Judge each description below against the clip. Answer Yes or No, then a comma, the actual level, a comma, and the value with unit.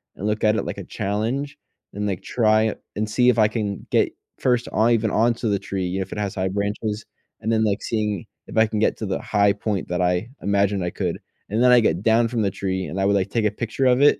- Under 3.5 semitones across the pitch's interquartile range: Yes, narrow, 2.4 semitones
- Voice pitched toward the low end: Yes, low, 105 Hz